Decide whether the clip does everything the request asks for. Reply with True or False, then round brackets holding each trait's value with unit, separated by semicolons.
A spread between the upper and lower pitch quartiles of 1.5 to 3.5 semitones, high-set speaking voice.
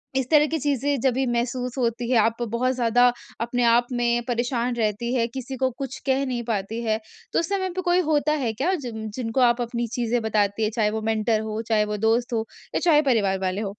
True (2.7 semitones; 240 Hz)